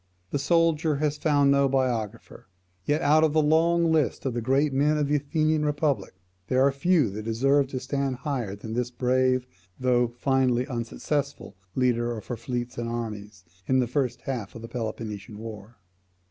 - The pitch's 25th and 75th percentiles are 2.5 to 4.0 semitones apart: Yes, average, 3.7 semitones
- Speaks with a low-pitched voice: Yes, low, 130 Hz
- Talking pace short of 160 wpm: No, average, 175 wpm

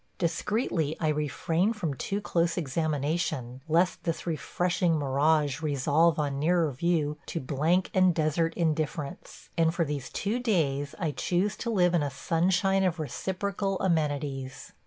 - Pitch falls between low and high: Yes, medium, 160 Hz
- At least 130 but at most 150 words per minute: Yes, average, 140 wpm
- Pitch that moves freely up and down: No, average, 3.5 semitones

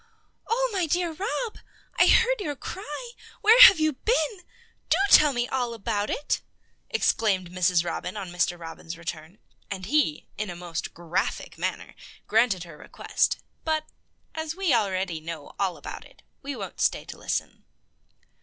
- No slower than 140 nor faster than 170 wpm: Yes, average, 155 wpm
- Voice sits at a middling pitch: No, high, 225 Hz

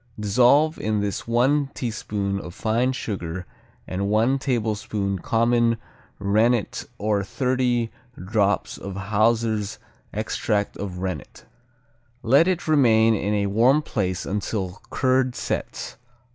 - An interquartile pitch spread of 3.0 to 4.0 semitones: Yes, average, 3.6 semitones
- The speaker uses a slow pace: Yes, slow, 115 wpm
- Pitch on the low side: Yes, low, 110 Hz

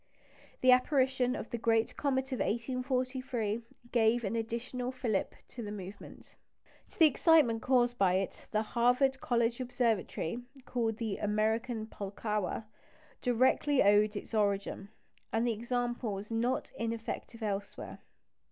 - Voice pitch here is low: No, high, 230 Hz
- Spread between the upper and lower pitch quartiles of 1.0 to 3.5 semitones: Yes, average, 2.8 semitones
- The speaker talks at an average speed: No, slow, 130 wpm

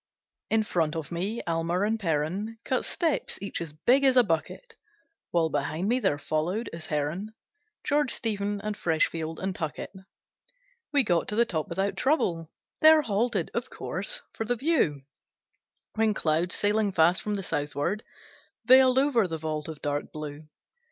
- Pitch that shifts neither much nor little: No, wide, 6.1 semitones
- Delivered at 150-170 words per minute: Yes, average, 160 wpm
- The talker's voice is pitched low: No, high, 195 Hz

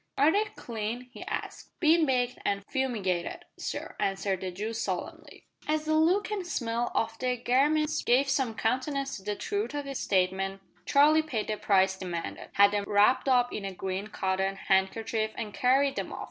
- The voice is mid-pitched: No, high, 235 Hz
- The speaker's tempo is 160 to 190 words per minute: Yes, average, 180 wpm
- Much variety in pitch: Yes, wide, 6.0 semitones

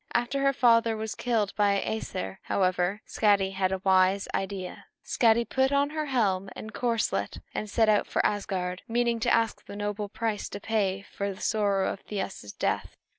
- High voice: Yes, high, 205 Hz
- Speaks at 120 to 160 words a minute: No, average, 180 wpm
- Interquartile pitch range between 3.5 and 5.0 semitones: No, average, 3.0 semitones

